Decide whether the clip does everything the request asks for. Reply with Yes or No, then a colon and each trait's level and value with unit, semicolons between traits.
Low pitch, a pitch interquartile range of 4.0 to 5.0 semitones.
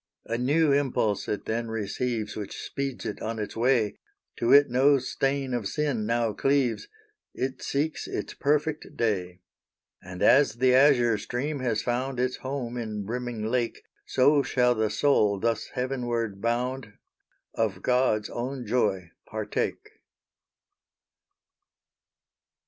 No: low, 120 Hz; average, 3.5 semitones